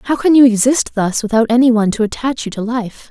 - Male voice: No, female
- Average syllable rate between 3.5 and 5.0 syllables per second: No, 5.9 syllables/s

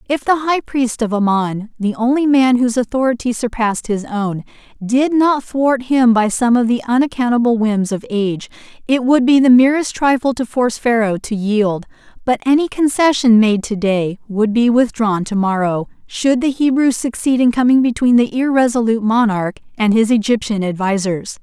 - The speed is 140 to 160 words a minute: No, average, 170 wpm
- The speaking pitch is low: No, high, 235 Hz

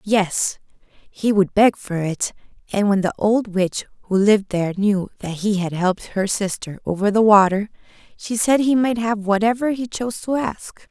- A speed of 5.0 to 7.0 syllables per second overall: No, 4.7 syllables/s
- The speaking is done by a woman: Yes, female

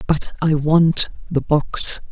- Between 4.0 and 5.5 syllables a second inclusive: No, 3.1 syllables/s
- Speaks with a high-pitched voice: No, medium, 155 Hz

